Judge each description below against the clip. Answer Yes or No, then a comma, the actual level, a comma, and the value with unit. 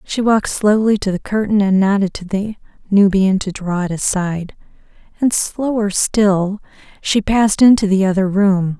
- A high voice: Yes, high, 200 Hz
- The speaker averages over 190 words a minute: No, average, 165 wpm